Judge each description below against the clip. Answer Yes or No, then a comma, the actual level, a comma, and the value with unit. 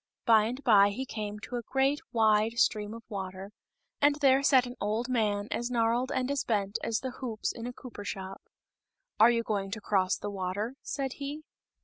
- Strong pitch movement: No, average, 3.7 semitones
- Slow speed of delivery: No, average, 200 wpm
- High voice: Yes, high, 230 Hz